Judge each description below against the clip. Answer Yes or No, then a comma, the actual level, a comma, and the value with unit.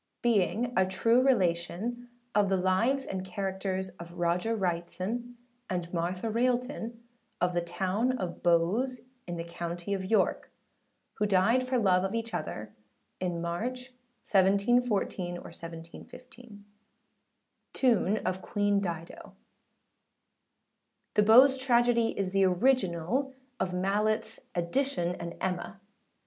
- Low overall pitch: No, high, 195 Hz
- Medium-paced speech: No, slow, 115 wpm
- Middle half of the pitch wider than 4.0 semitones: Yes, average, 5.2 semitones